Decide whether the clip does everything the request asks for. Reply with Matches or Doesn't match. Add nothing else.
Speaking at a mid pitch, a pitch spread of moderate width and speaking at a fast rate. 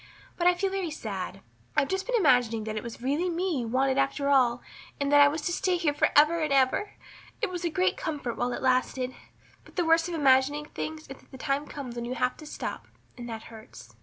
Doesn't match